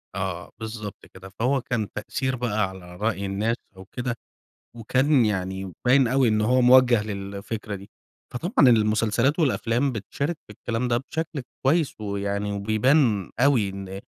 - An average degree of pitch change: Yes, average, 4.2 semitones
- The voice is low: Yes, low, 110 Hz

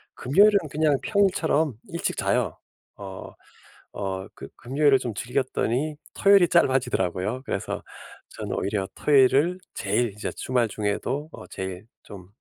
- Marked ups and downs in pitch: Yes, wide, 6.9 semitones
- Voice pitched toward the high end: No, low, 130 Hz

